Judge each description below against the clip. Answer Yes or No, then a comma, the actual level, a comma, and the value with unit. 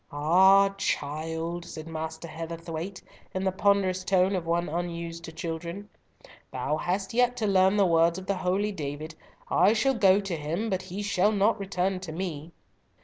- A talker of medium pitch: Yes, medium, 180 Hz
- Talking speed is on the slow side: No, average, 170 wpm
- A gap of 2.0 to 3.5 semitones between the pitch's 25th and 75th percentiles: Yes, average, 3.1 semitones